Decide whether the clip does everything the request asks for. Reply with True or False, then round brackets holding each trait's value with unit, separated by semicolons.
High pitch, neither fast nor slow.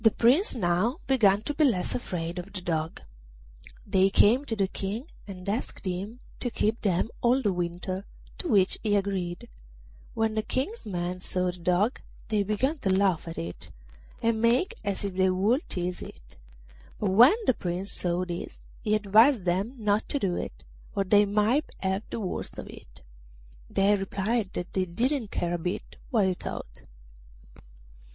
True (200 Hz; 175 wpm)